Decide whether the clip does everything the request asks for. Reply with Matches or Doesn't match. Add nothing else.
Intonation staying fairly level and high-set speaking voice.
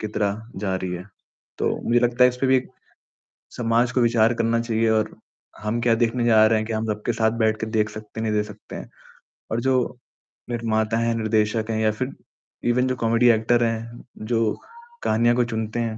Doesn't match